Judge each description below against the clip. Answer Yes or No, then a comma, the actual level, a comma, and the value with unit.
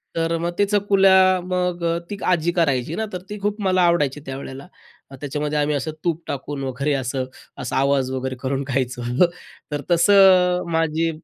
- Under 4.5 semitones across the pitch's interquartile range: No, average, 4.9 semitones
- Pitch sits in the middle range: Yes, medium, 165 Hz